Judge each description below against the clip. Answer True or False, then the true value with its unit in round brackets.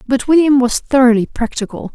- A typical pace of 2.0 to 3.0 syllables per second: False (5.7 syllables/s)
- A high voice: True (255 Hz)